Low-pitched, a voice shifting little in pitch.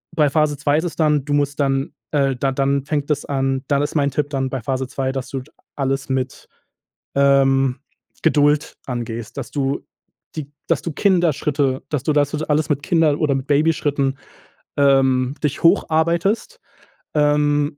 No: medium, 145 Hz; narrow, 1.9 semitones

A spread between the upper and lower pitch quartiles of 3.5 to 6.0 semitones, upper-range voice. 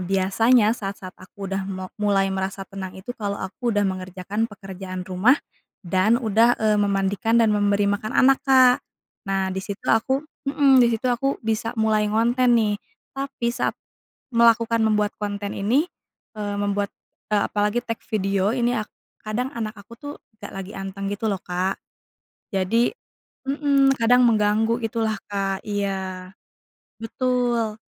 No: average, 3.1 semitones; high, 210 Hz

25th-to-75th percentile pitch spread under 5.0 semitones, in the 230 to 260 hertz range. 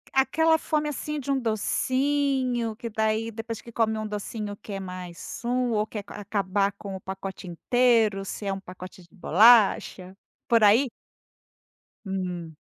No: average, 3.9 semitones; high, 215 Hz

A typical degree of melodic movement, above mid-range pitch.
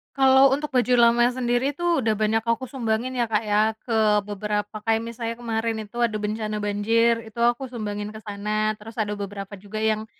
No: narrow, 2.2 semitones; high, 220 Hz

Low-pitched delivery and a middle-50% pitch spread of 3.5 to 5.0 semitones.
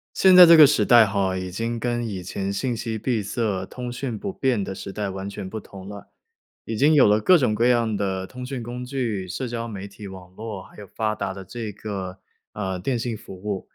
Yes: low, 110 Hz; average, 3.9 semitones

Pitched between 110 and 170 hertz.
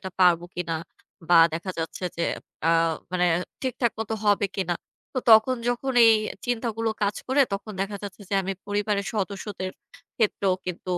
No: high, 200 Hz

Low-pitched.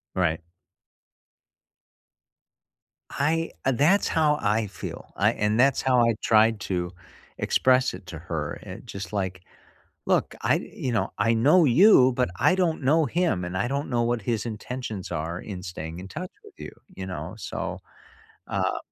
Yes: low, 115 Hz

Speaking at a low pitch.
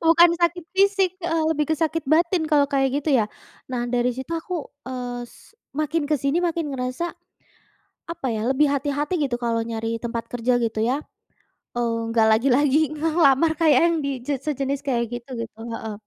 No: very high, 280 Hz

